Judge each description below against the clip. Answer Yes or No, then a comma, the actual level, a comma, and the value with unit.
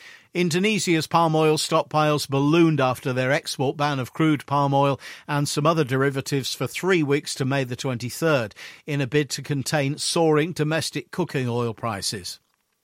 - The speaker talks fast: No, average, 160 wpm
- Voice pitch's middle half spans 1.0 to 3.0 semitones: Yes, average, 2.7 semitones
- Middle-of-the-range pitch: Yes, medium, 145 Hz